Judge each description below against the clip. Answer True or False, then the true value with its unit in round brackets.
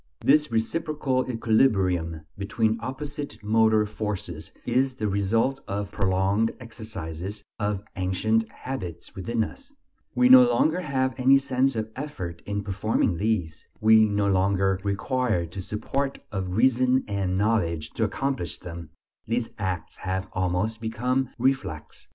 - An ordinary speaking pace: False (130 wpm)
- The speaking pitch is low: True (110 Hz)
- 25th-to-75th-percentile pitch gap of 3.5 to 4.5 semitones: False (5.2 semitones)